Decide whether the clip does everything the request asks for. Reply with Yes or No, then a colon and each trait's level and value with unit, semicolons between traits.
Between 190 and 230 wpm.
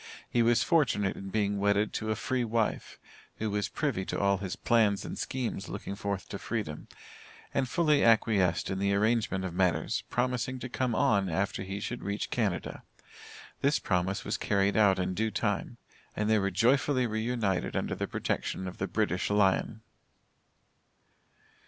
No: average, 170 wpm